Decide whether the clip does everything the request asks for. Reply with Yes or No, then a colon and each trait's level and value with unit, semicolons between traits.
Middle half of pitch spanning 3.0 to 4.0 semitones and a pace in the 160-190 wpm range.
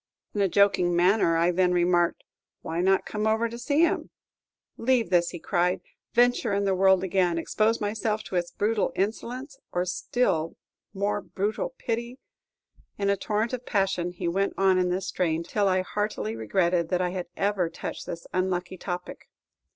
Yes: average, 3.4 semitones; average, 175 wpm